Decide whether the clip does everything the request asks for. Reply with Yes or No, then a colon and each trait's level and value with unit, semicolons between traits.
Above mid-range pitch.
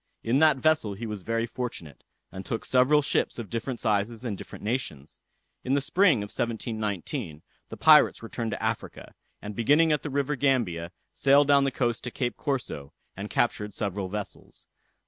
No: low, 115 Hz